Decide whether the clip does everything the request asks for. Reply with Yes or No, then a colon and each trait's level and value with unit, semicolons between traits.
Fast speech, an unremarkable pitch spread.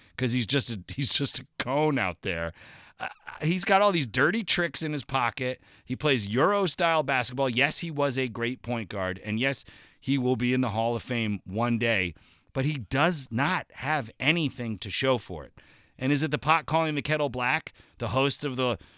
Yes: fast, 210 wpm; average, 4.2 semitones